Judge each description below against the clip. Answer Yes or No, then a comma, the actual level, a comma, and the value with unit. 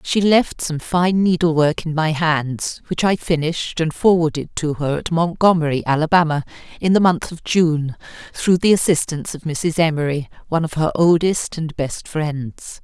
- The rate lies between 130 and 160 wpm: No, average, 175 wpm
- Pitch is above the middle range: No, medium, 160 Hz